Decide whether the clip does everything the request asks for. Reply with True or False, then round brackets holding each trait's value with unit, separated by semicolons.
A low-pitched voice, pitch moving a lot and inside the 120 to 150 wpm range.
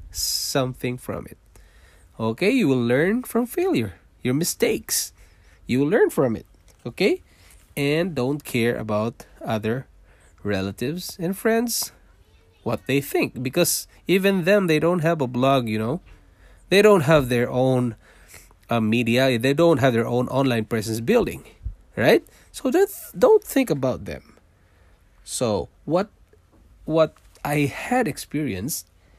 True (125 Hz; 8.9 semitones; 140 wpm)